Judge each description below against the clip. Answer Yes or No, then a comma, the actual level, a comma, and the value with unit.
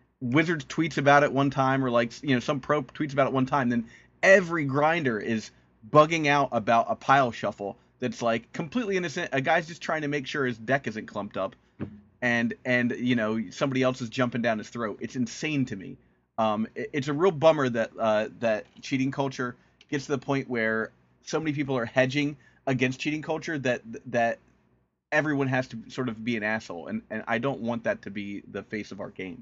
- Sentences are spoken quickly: Yes, fast, 215 wpm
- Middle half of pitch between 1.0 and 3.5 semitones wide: No, average, 4.1 semitones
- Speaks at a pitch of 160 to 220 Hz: No, low, 130 Hz